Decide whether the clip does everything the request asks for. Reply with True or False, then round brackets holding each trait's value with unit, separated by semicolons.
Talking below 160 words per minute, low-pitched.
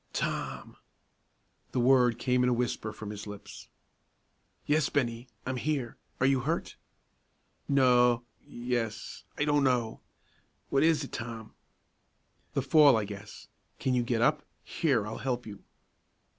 True (140 wpm; 125 Hz)